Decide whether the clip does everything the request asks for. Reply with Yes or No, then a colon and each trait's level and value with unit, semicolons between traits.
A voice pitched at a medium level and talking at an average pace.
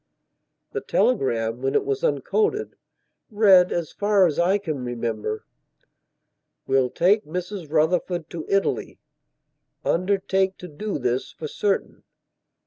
No: medium, 170 Hz; slow, 120 wpm